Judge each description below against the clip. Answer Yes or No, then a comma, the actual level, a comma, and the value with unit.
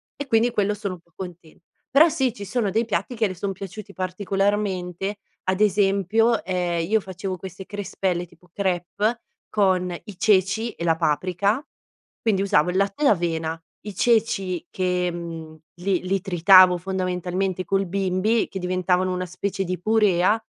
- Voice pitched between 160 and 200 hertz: Yes, high, 190 Hz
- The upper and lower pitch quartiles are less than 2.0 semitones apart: No, narrow, 2.4 semitones